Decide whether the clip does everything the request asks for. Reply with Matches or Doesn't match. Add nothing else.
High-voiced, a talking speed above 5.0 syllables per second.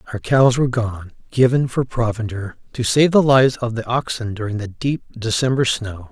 Doesn't match